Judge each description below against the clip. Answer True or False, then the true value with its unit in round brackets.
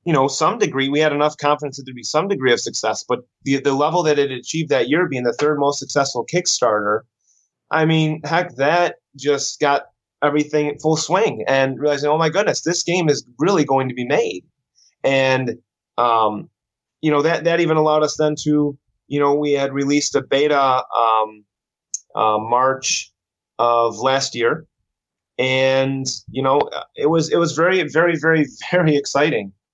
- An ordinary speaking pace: True (180 wpm)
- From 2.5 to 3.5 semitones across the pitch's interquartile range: True (3.0 semitones)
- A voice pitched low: False (145 Hz)